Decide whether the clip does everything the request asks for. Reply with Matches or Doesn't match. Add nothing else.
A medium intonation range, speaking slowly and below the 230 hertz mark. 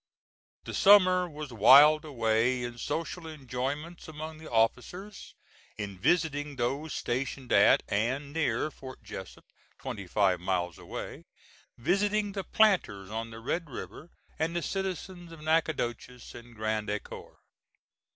Doesn't match